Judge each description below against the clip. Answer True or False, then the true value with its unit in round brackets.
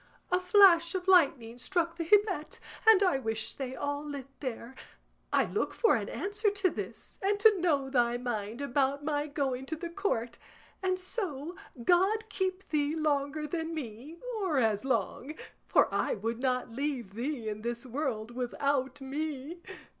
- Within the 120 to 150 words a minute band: False (160 wpm)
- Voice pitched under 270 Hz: False (285 Hz)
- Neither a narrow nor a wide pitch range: False (6.0 semitones)